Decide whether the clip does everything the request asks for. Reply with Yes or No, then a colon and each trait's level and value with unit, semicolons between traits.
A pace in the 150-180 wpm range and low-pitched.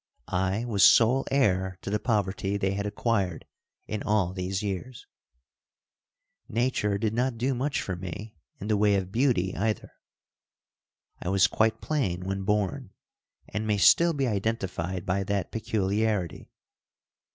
No: average, 140 wpm; low, 105 Hz